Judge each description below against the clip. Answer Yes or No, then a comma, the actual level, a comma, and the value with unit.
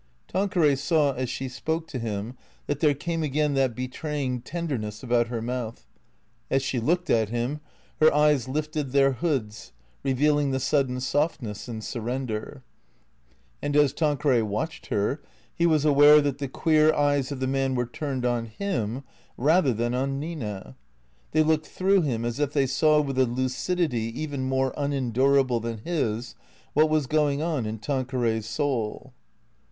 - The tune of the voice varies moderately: Yes, average, 3.7 semitones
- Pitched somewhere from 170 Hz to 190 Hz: No, low, 135 Hz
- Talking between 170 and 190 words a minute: No, average, 160 wpm